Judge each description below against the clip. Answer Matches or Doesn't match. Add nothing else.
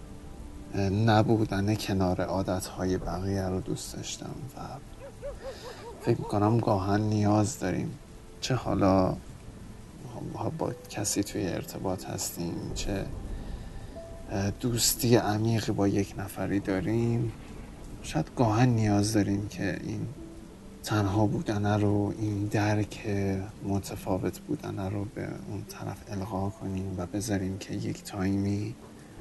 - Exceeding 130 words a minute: Doesn't match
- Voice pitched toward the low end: Matches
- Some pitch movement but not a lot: Doesn't match